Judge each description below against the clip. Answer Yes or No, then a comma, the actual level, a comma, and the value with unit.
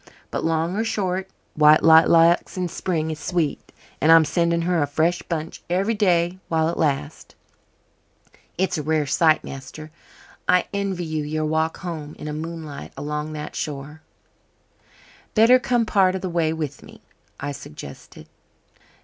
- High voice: No, medium, 160 Hz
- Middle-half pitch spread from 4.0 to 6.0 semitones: No, average, 2.7 semitones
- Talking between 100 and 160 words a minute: Yes, average, 155 wpm